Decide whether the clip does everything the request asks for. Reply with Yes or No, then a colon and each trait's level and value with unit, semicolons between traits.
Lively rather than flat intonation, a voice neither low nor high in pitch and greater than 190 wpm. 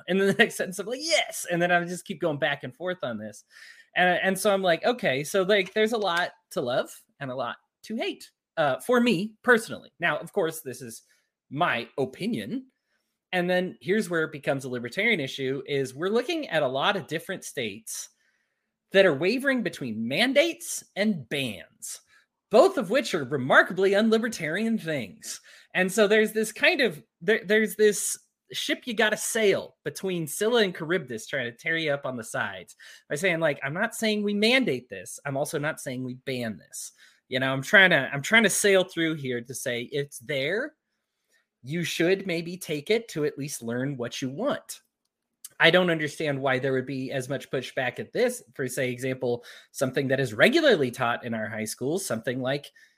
Yes: wide, 7.9 semitones; medium, 175 Hz; average, 200 wpm